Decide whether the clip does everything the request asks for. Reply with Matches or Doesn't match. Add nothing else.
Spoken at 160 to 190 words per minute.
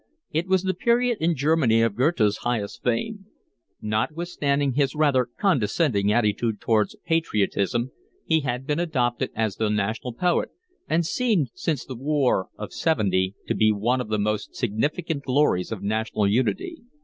Doesn't match